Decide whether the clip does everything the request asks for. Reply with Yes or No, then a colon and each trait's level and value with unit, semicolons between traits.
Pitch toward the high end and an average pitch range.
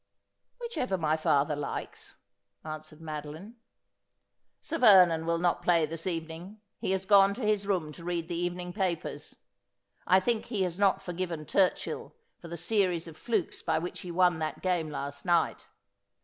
No: medium, 175 Hz; average, 3.1 semitones